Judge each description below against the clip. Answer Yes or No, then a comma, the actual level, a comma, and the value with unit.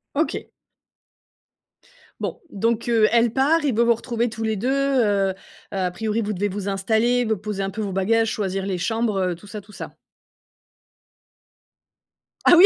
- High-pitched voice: Yes, high, 220 Hz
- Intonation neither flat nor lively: Yes, average, 3.1 semitones